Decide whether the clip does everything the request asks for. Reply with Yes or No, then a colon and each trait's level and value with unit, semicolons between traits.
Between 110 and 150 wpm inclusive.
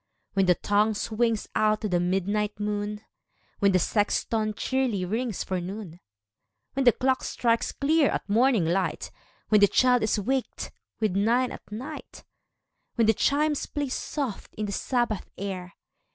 No: average, 170 wpm